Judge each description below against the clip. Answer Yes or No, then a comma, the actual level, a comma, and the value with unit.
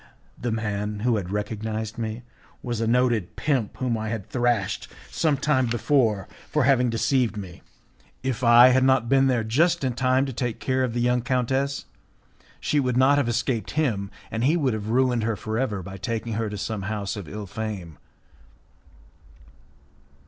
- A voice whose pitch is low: Yes, low, 115 Hz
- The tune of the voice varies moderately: Yes, average, 3.3 semitones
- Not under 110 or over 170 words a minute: No, average, 180 wpm